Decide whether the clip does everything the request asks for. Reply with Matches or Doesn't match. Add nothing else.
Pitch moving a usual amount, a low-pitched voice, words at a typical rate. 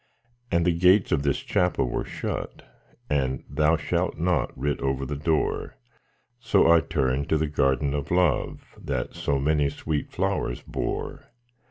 Matches